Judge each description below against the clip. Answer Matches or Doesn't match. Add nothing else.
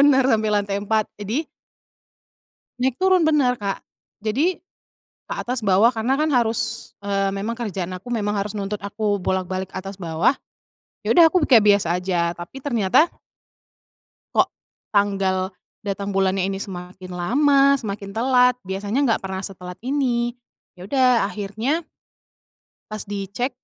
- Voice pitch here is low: Doesn't match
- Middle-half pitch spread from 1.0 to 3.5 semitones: Doesn't match